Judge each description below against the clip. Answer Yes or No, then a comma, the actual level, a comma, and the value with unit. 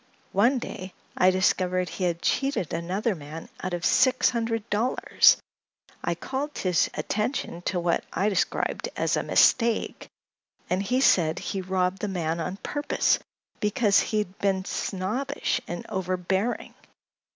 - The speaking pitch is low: No, high, 190 Hz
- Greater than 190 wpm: No, average, 140 wpm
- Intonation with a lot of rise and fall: No, average, 4.1 semitones